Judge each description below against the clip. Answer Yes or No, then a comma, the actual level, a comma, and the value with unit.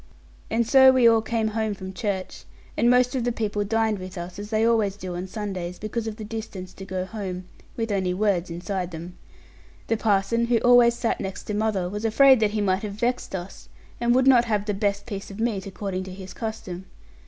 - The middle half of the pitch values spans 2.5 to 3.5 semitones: Yes, average, 3.1 semitones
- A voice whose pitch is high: Yes, high, 210 Hz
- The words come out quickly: Yes, fast, 220 wpm